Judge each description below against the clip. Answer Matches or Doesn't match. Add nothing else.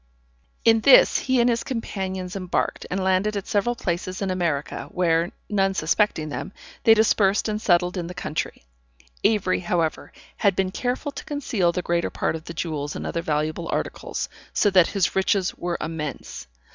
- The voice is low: Doesn't match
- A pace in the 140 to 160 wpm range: Doesn't match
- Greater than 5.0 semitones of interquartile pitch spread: Doesn't match